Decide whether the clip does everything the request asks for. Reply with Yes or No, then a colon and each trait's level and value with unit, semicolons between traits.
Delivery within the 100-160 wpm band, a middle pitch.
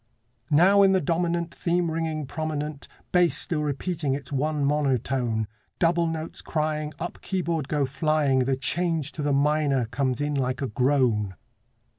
Yes: average, 150 wpm; medium, 150 Hz